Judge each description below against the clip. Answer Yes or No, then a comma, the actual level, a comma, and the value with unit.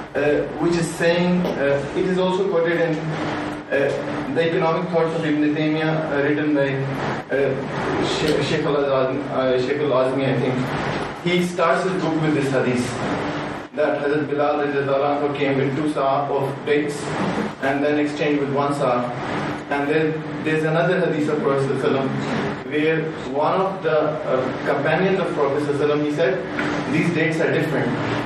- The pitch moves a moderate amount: No, narrow, 2.3 semitones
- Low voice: No, medium, 150 Hz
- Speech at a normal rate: No, fast, 150 wpm